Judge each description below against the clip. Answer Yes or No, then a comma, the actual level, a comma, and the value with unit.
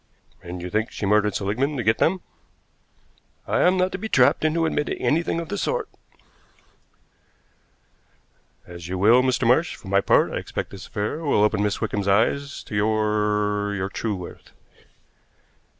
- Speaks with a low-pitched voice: Yes, low, 105 Hz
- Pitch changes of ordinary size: No, wide, 5.7 semitones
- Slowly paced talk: No, average, 165 wpm